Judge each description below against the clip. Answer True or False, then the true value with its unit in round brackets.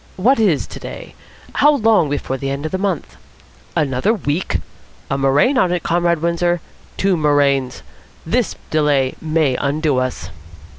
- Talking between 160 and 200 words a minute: False (145 wpm)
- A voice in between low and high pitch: True (155 Hz)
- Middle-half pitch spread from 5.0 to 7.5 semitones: False (4.5 semitones)